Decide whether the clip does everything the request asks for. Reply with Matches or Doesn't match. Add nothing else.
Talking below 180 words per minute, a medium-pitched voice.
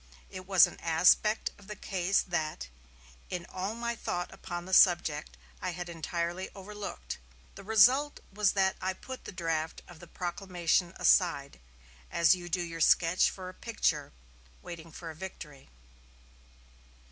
Matches